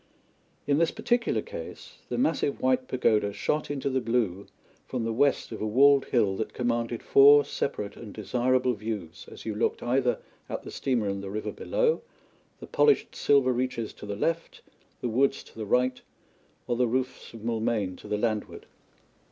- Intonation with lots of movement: No, average, 3.9 semitones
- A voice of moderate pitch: No, low, 120 Hz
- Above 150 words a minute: Yes, average, 175 wpm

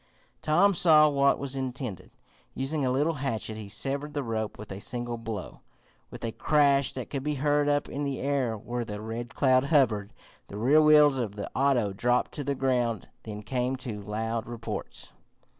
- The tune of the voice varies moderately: Yes, average, 4.0 semitones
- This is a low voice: Yes, low, 130 Hz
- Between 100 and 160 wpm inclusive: No, average, 185 wpm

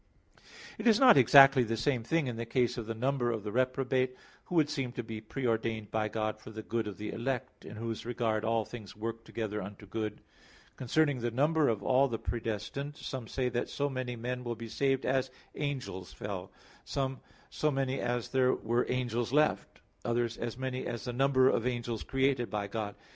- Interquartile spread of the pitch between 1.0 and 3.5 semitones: Yes, average, 2.9 semitones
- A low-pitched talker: Yes, low, 120 Hz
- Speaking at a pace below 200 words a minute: No, fast, 205 wpm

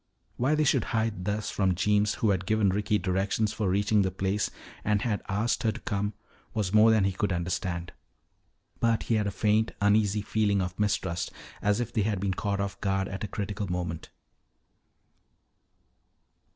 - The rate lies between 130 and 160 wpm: No, average, 180 wpm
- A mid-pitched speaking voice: No, low, 100 Hz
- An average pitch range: No, narrow, 2.0 semitones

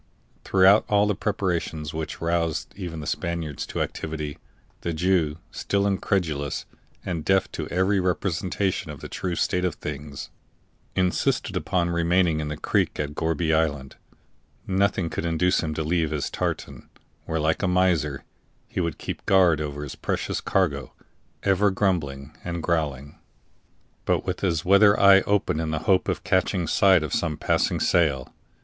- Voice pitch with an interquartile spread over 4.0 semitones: No, average, 3.4 semitones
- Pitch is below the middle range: Yes, very low, 85 Hz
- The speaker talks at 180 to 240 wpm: No, average, 155 wpm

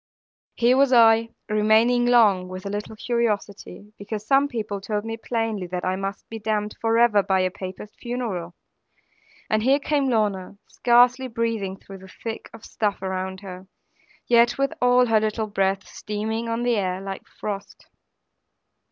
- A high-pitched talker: Yes, high, 215 Hz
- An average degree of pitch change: Yes, average, 3.2 semitones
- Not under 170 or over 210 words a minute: No, average, 160 wpm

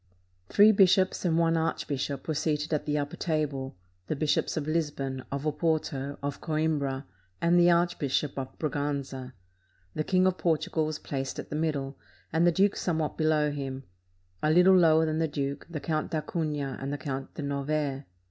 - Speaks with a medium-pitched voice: Yes, medium, 150 Hz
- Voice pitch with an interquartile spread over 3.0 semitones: No, narrow, 2.5 semitones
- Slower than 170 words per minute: No, average, 175 wpm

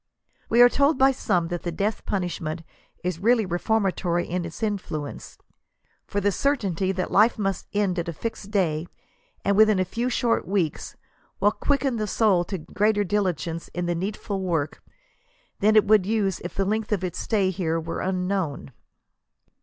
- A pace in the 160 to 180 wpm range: Yes, average, 170 wpm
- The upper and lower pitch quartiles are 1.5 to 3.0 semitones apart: No, average, 3.6 semitones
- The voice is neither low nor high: No, high, 195 Hz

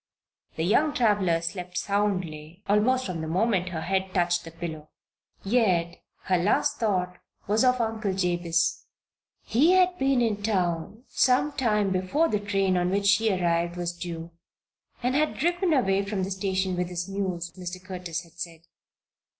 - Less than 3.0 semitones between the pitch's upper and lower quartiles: No, average, 3.8 semitones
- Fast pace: No, average, 160 wpm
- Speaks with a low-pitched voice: No, high, 190 Hz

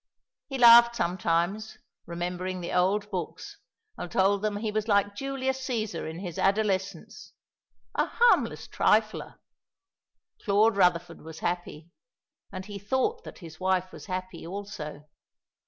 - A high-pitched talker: Yes, high, 195 Hz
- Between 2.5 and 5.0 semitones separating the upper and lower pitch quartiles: Yes, average, 3.5 semitones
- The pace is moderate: No, slow, 130 wpm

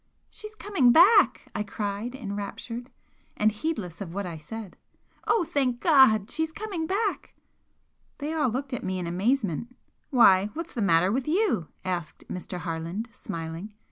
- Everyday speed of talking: Yes, average, 150 wpm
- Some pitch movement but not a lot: No, wide, 8.2 semitones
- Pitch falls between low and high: No, high, 225 Hz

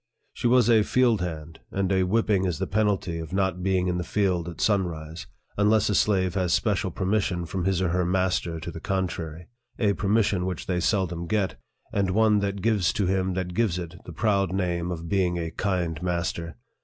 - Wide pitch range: No, narrow, 2.6 semitones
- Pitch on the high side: No, very low, 95 Hz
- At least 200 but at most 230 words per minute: Yes, fast, 205 wpm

